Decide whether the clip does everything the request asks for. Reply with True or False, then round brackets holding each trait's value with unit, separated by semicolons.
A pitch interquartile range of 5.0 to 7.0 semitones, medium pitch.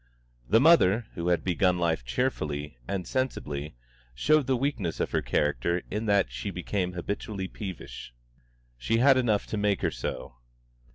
False (5.3 semitones; 95 Hz)